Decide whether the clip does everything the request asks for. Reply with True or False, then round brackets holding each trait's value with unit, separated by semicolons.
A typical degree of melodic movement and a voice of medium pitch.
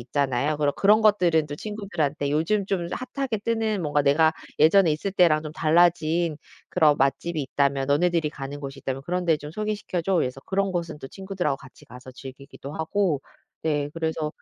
True (4.2 semitones; 160 Hz)